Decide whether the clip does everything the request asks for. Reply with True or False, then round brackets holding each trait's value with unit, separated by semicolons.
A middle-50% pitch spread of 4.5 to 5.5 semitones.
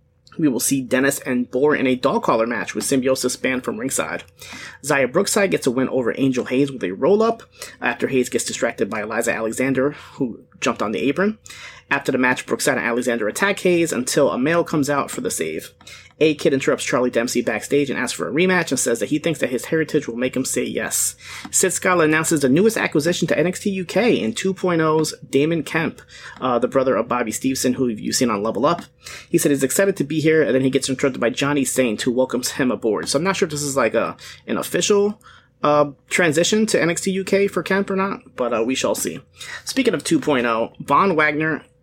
True (5.2 semitones)